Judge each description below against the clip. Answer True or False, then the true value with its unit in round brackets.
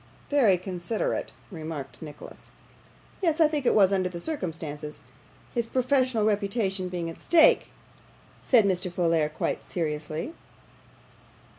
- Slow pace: True (120 wpm)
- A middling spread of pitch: False (6.5 semitones)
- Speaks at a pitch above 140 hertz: True (185 Hz)